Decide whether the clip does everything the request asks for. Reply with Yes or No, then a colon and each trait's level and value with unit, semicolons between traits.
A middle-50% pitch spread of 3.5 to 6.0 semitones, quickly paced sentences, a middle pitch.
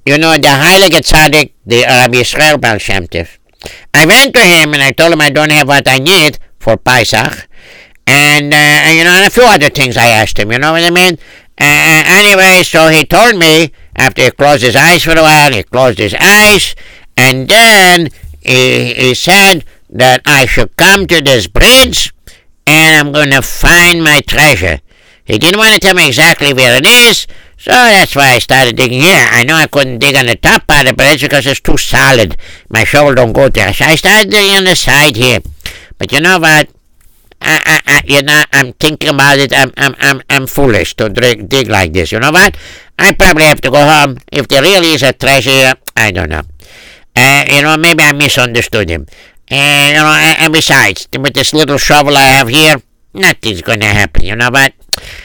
Yes: average, 4.1 semitones; fast, 210 wpm; medium, 145 Hz